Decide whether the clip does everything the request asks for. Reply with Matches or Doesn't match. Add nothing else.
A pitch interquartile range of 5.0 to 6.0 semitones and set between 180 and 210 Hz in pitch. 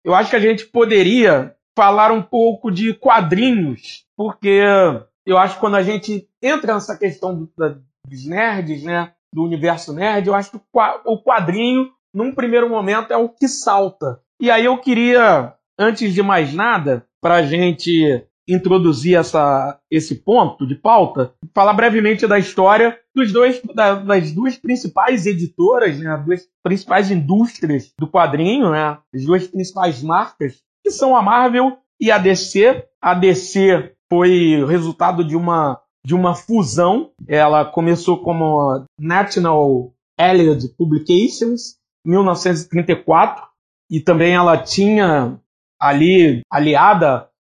Matches